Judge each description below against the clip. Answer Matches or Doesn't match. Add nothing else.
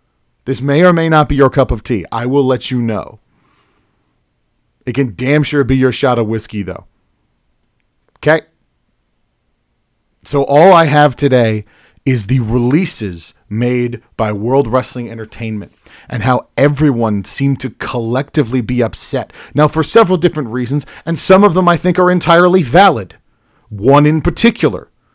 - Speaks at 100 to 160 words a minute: Matches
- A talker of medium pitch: Doesn't match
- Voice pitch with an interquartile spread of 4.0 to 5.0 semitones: Matches